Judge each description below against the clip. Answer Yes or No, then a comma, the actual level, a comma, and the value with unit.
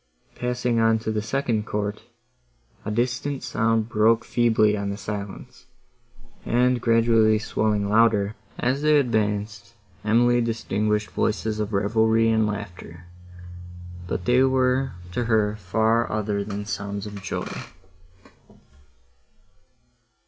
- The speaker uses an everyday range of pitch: No, narrow, 2.1 semitones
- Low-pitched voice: Yes, low, 110 Hz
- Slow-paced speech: Yes, slow, 115 wpm